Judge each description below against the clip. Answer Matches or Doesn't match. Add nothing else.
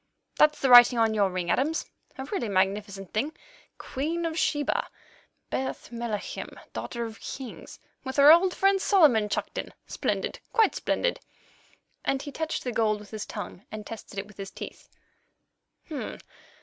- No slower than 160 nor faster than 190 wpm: Doesn't match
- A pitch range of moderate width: Doesn't match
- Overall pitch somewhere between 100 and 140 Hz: Doesn't match